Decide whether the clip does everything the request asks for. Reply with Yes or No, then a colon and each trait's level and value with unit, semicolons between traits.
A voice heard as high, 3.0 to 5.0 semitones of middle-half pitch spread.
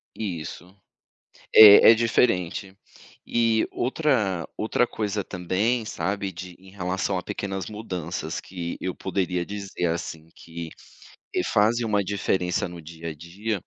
No: very low, 95 Hz; average, 3.3 semitones